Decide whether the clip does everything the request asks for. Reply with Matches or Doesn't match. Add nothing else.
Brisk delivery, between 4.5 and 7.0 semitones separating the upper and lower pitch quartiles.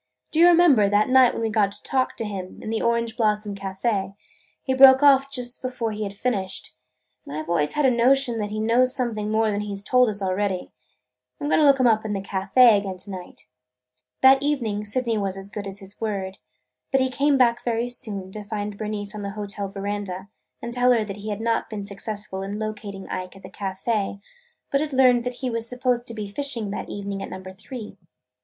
Doesn't match